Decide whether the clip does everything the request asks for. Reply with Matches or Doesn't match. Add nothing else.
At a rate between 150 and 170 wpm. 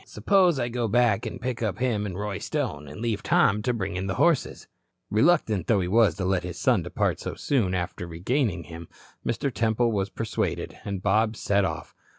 Doesn't match